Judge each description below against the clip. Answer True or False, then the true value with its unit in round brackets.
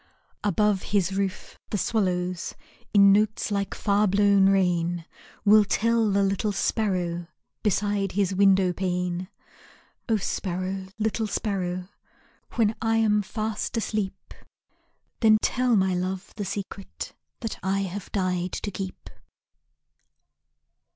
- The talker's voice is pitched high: True (195 Hz)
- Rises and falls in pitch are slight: True (2.2 semitones)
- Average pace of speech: False (115 wpm)